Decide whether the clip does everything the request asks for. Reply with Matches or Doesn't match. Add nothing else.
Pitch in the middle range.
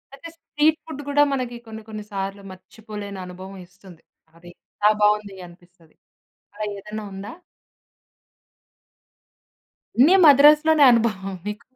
Doesn't match